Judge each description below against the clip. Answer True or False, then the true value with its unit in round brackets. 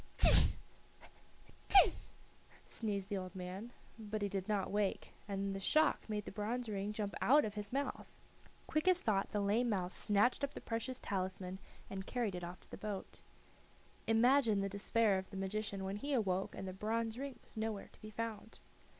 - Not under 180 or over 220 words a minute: True (185 wpm)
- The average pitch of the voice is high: True (210 Hz)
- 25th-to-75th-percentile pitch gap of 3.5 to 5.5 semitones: False (2.7 semitones)